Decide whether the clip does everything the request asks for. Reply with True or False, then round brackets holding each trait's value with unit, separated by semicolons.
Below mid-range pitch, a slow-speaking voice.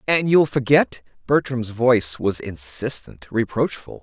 True (120 Hz; 120 wpm)